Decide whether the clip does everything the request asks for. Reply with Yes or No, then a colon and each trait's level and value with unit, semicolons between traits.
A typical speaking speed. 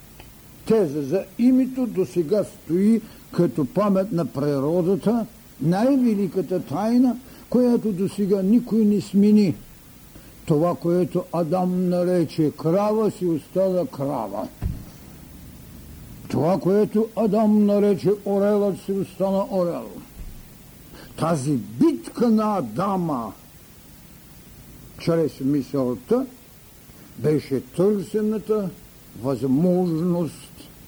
No: slow, 85 wpm